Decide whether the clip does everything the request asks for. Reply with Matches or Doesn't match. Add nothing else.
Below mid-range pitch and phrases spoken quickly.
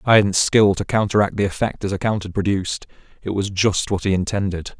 Matches